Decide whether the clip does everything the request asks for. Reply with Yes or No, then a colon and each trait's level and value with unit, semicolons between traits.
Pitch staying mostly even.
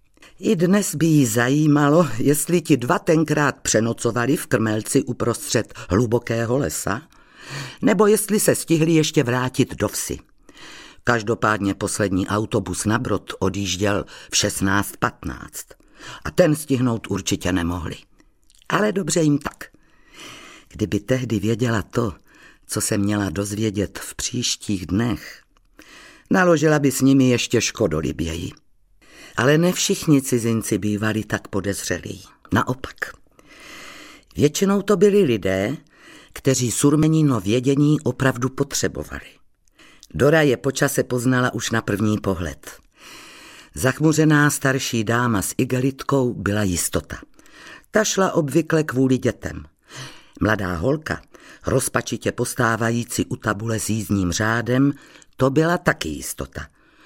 No: wide, 5.7 semitones